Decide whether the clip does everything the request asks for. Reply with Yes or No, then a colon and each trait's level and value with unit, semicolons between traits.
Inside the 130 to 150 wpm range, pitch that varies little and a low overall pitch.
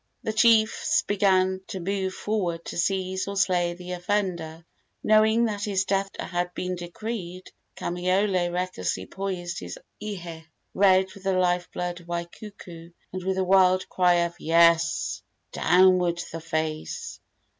No: average, 140 wpm; narrow, 2.1 semitones; medium, 185 Hz